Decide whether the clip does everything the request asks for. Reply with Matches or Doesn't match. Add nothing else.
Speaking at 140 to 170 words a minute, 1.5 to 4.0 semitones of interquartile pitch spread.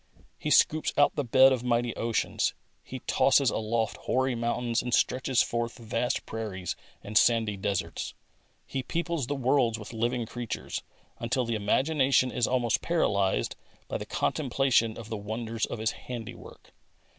Matches